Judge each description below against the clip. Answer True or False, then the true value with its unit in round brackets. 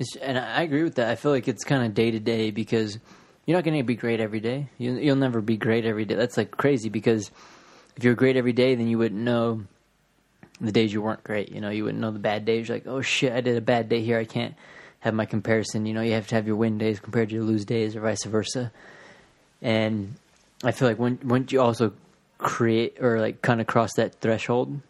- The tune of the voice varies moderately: False (2.1 semitones)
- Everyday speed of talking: False (245 wpm)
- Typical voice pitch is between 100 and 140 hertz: True (115 Hz)